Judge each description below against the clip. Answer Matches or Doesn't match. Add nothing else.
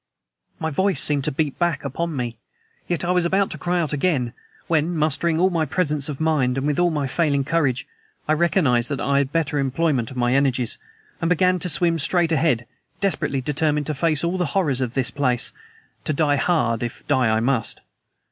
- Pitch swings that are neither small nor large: Matches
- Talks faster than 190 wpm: Matches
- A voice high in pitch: Doesn't match